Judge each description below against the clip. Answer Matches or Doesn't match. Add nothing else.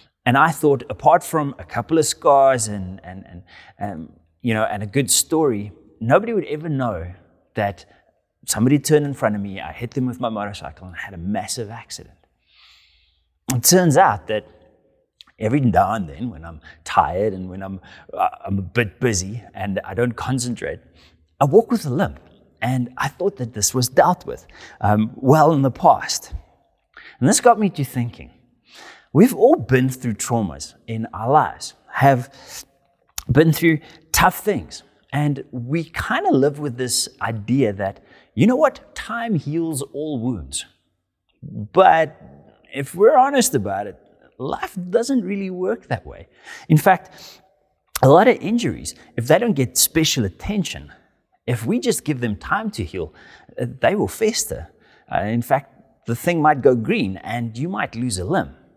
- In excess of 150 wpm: Matches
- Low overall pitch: Matches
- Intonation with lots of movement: Matches